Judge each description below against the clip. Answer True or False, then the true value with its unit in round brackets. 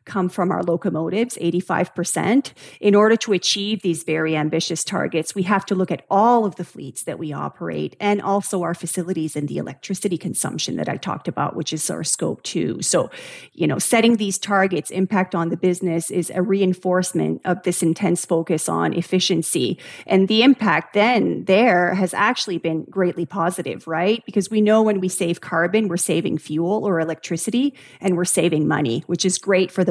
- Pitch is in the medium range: True (180 Hz)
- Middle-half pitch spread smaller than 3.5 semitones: True (3.0 semitones)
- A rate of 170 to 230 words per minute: True (185 wpm)